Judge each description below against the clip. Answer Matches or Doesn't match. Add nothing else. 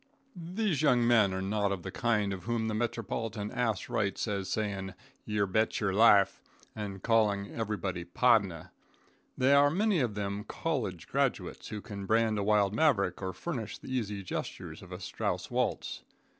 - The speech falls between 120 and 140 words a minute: Doesn't match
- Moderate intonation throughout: Matches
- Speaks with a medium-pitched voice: Doesn't match